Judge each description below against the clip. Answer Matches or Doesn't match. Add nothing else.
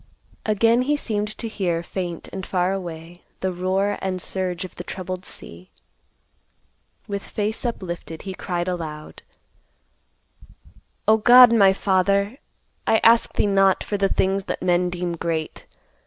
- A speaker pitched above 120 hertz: Matches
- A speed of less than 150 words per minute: Matches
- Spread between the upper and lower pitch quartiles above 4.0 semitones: Doesn't match